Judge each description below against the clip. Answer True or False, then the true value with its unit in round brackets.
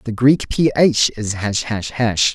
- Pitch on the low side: True (115 Hz)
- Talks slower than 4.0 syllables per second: True (3.7 syllables/s)